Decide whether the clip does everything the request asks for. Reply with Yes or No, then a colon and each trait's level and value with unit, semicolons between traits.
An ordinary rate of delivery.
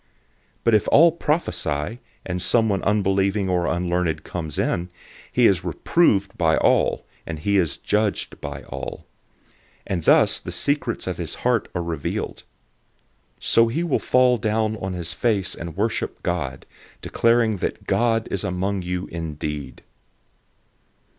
Yes: average, 145 wpm